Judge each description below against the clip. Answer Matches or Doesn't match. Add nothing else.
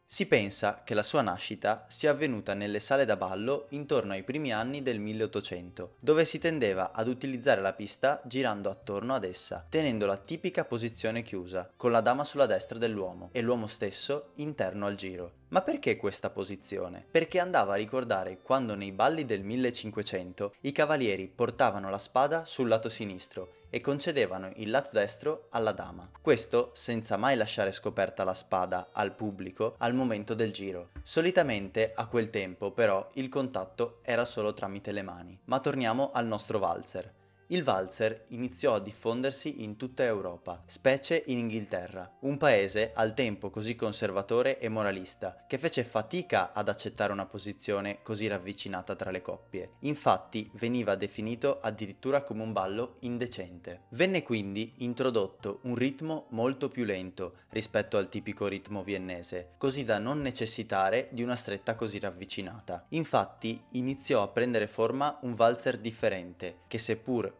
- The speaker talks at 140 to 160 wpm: Matches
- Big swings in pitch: Doesn't match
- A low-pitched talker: Matches